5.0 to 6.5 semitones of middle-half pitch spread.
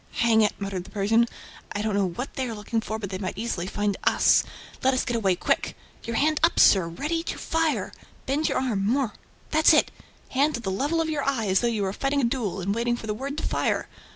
Yes: wide, 5.4 semitones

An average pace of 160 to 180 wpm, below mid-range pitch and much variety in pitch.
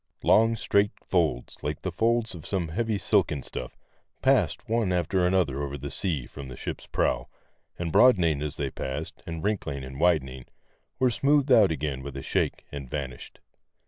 Yes: average, 175 wpm; very low, 80 Hz; wide, 6.4 semitones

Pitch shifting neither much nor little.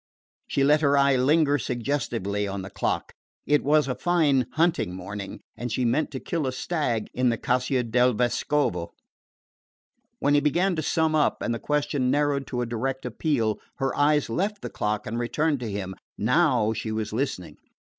Yes: average, 4.4 semitones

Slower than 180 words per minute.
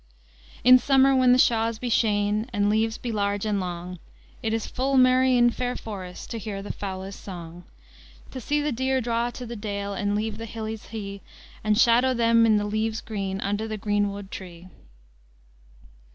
No: average, 185 wpm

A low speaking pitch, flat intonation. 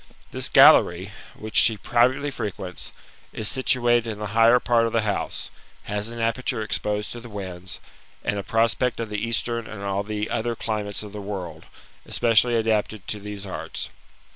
Yes: low, 110 Hz; narrow, 2.3 semitones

